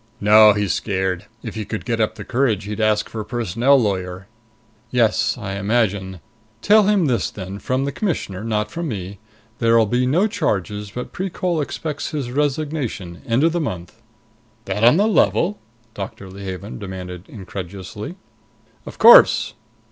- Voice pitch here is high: No, low, 110 Hz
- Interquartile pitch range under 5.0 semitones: No, wide, 5.6 semitones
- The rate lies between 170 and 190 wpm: No, average, 155 wpm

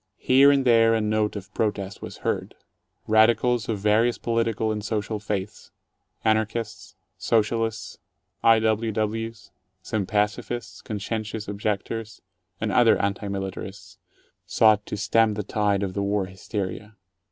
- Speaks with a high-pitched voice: No, low, 110 Hz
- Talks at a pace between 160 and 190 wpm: No, average, 140 wpm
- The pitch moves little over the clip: Yes, narrow, 1.7 semitones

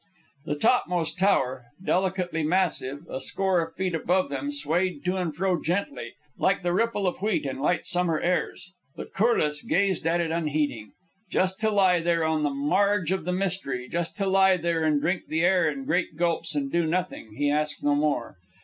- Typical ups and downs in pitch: Yes, average, 3.7 semitones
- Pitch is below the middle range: No, medium, 175 Hz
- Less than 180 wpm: No, average, 190 wpm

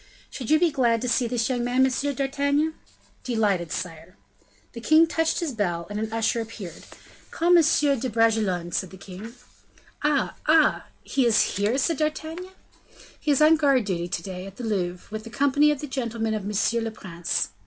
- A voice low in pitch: No, high, 235 Hz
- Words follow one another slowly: No, average, 185 wpm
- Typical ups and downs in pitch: No, wide, 5.8 semitones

